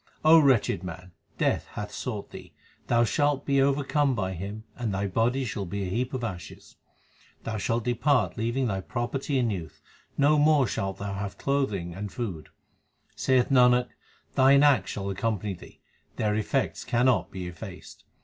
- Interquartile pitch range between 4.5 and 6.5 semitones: Yes, average, 5.2 semitones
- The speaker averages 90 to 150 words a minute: No, average, 165 wpm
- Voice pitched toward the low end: Yes, low, 115 Hz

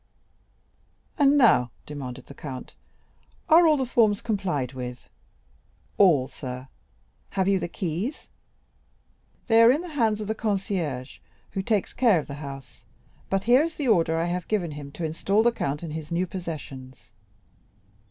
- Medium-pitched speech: Yes, medium, 180 Hz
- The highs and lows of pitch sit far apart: Yes, wide, 7.5 semitones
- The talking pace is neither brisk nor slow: Yes, average, 160 wpm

